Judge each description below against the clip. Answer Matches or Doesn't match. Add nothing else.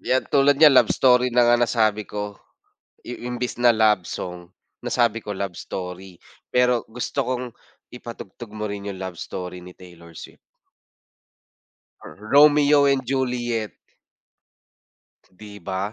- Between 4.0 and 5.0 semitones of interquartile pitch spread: Matches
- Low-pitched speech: Matches